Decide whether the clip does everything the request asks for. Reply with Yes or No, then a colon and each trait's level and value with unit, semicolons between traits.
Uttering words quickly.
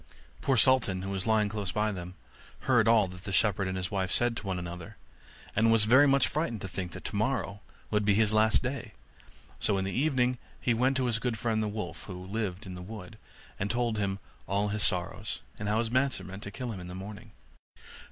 Yes: fast, 220 wpm